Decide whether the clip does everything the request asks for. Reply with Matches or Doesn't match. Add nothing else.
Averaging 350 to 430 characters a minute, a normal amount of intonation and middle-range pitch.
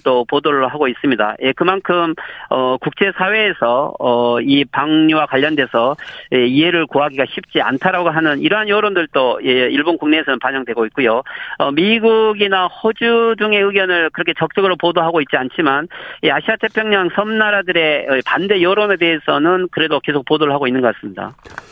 Doesn't match